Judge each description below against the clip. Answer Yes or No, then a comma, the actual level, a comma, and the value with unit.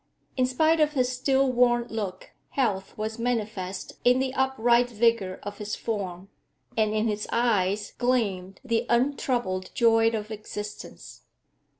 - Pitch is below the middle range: No, high, 225 Hz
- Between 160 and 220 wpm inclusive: No, slow, 135 wpm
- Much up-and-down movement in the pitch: No, average, 3.2 semitones